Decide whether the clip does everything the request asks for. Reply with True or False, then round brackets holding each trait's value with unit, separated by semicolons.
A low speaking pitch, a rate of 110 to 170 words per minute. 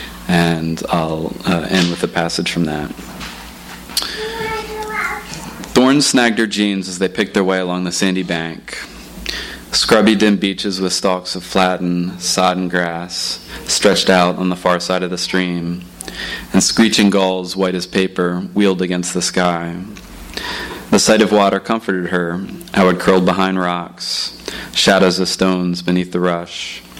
True (90 Hz; 150 wpm)